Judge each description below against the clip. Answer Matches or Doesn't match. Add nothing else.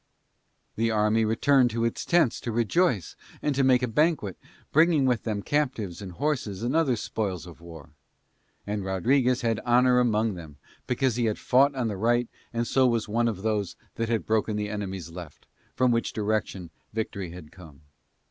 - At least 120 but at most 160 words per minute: Doesn't match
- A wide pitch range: Doesn't match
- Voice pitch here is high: Doesn't match